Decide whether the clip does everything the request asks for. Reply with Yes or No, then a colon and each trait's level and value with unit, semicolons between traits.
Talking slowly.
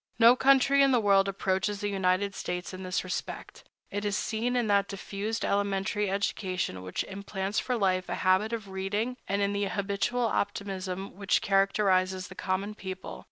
No: average, 170 wpm